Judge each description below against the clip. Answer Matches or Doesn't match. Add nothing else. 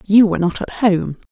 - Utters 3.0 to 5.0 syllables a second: Doesn't match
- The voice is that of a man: Doesn't match